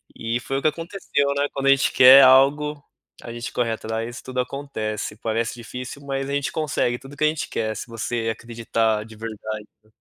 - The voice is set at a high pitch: No, low, 125 Hz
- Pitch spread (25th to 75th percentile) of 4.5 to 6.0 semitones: No, average, 3.6 semitones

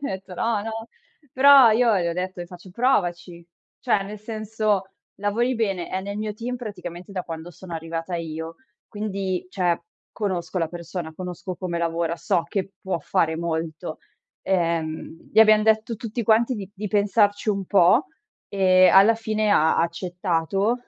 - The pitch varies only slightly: No, average, 3.9 semitones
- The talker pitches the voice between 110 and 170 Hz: No, high, 190 Hz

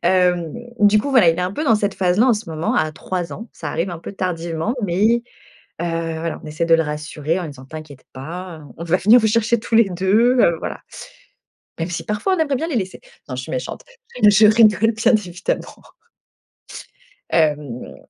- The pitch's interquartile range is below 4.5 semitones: No, average, 4.8 semitones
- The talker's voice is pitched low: No, medium, 180 Hz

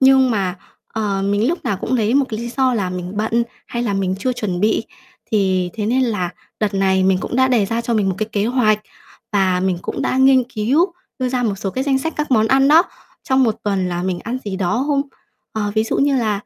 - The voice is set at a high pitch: Yes, high, 220 Hz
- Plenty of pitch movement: No, average, 4.7 semitones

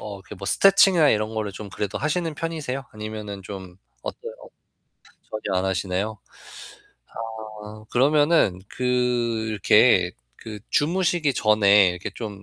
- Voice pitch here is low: Yes, low, 110 Hz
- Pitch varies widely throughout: Yes, wide, 6.7 semitones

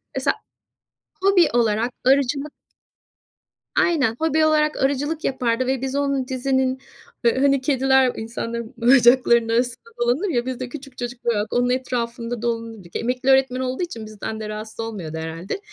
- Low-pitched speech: No, very high, 250 Hz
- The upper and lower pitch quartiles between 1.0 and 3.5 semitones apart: Yes, average, 2.8 semitones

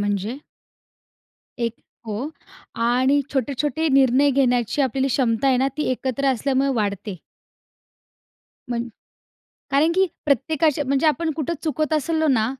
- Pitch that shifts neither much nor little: Yes, average, 3.6 semitones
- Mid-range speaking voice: No, very high, 265 Hz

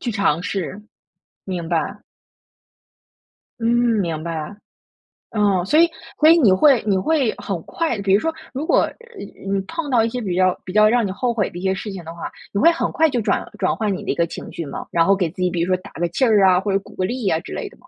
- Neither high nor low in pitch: No, high, 200 Hz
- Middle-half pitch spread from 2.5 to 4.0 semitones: No, average, 4.8 semitones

